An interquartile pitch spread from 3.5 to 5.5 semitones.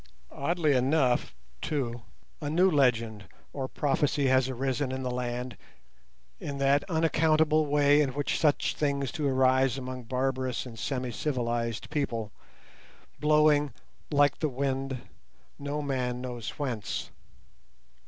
No: narrow, 2.6 semitones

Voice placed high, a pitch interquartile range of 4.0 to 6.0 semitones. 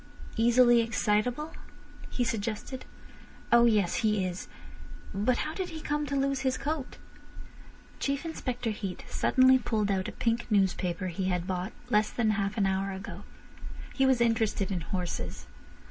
Yes: high, 225 Hz; average, 4.7 semitones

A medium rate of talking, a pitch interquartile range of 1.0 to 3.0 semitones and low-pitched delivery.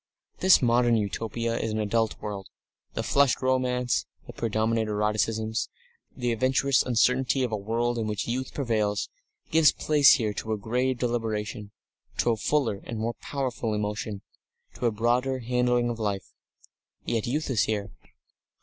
Yes: average, 150 wpm; average, 2.7 semitones; low, 115 Hz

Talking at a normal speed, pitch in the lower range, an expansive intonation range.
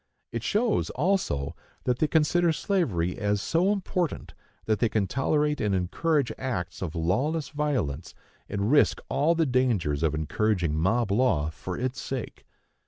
Yes: average, 150 wpm; low, 120 Hz; wide, 8.8 semitones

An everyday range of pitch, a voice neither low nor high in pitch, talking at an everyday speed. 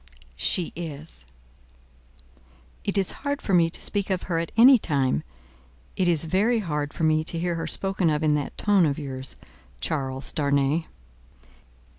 Yes: average, 4.3 semitones; medium, 165 Hz; average, 160 wpm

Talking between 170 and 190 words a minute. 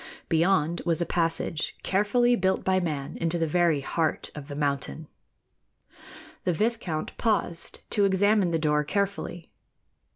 No: slow, 135 wpm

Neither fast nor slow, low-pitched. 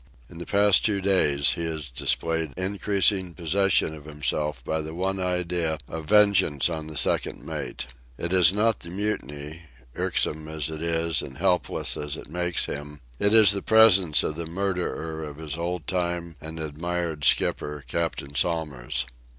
Yes: average, 165 wpm; very low, 85 Hz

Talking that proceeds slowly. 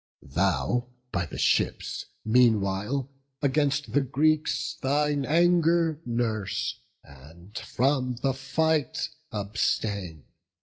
Yes: slow, 90 wpm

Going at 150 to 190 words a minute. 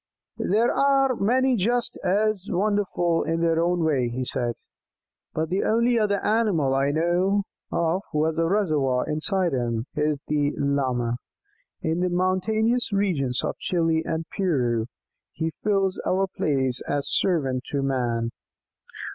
No: average, 140 wpm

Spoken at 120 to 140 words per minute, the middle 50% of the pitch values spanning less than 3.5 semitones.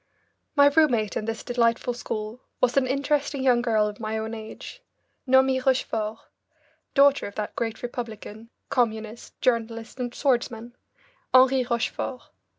Yes: slow, 135 wpm; average, 2.9 semitones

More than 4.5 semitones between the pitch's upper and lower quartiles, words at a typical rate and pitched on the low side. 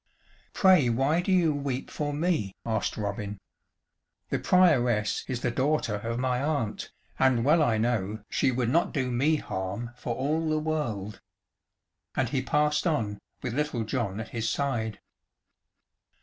Yes: average, 5.0 semitones; average, 150 wpm; low, 125 Hz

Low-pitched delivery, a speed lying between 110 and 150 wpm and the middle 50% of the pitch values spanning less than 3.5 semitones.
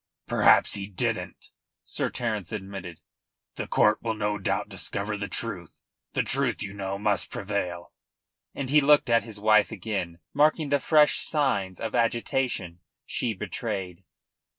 No: low, 105 Hz; average, 145 wpm; average, 3.8 semitones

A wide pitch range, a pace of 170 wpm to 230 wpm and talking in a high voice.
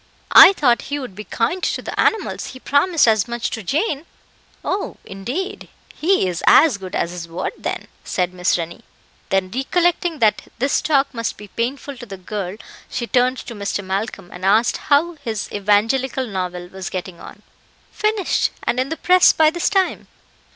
Yes: wide, 7.2 semitones; average, 180 wpm; high, 235 Hz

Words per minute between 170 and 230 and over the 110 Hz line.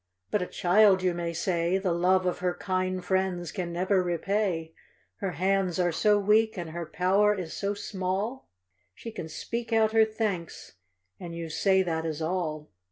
Yes: average, 175 wpm; medium, 185 Hz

